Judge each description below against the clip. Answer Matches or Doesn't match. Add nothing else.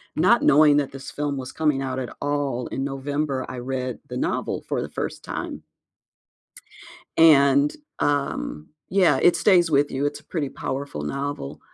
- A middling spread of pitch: Doesn't match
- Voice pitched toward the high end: Doesn't match